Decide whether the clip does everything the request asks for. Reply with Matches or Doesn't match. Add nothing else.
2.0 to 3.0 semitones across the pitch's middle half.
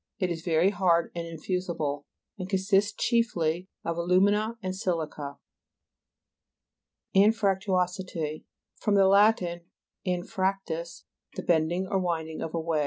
Matches